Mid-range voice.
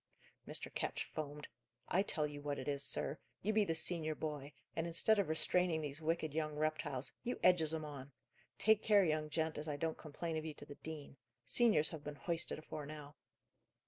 Yes: medium, 155 Hz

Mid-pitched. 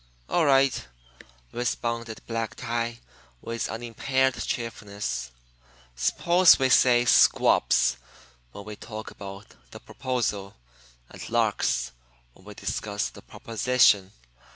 No: low, 115 Hz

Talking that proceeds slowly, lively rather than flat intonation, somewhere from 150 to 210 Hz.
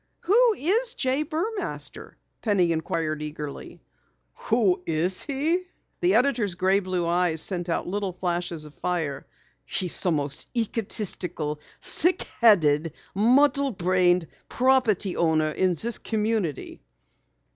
Yes: slow, 115 wpm; wide, 7.1 semitones; medium, 185 Hz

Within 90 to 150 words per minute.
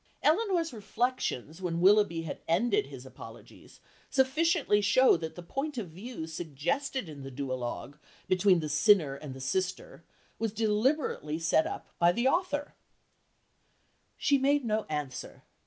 Yes: average, 140 wpm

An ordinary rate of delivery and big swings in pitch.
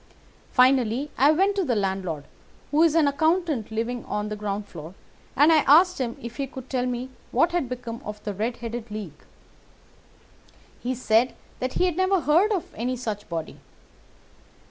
Yes: average, 175 wpm; wide, 5.9 semitones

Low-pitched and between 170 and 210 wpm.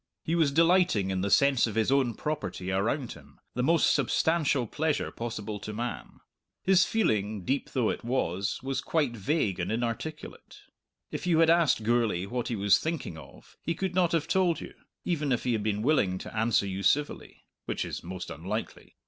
Yes: low, 120 Hz; average, 190 wpm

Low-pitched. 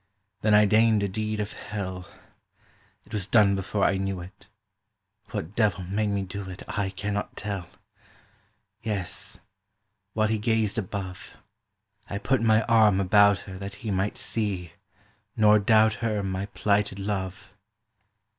Yes: low, 100 Hz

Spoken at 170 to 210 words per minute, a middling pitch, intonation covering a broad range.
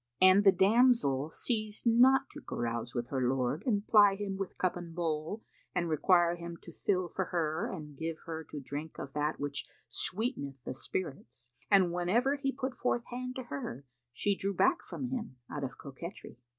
Yes: average, 190 wpm; medium, 175 Hz; wide, 6.7 semitones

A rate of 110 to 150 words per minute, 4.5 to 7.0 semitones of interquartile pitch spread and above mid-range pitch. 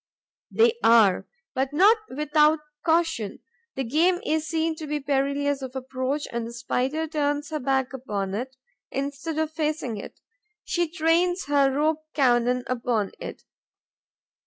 No: average, 140 wpm; average, 3.7 semitones; very high, 285 Hz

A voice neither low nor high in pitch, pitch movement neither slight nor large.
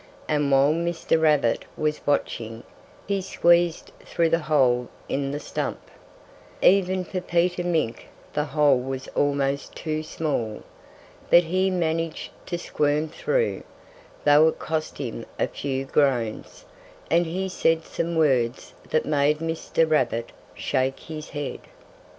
Yes: medium, 155 Hz; average, 3.5 semitones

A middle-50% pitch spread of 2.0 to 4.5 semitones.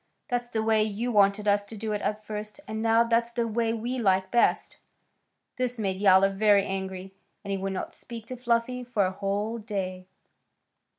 Yes: average, 2.8 semitones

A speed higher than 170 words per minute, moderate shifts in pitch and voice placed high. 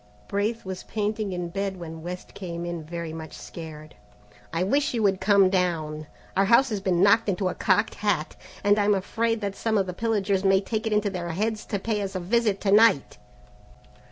Yes: fast, 205 wpm; average, 3.2 semitones; high, 195 Hz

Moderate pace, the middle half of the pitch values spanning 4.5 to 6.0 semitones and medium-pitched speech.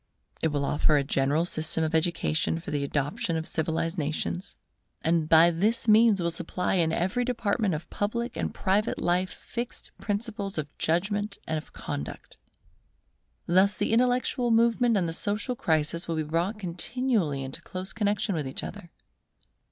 Yes: average, 165 wpm; average, 4.9 semitones; medium, 175 Hz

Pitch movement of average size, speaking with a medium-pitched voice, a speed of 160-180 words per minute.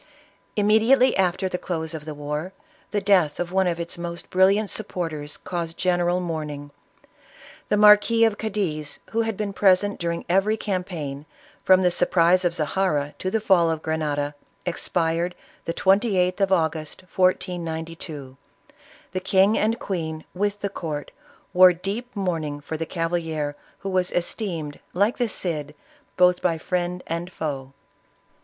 No: average, 3.3 semitones; medium, 180 Hz; average, 150 wpm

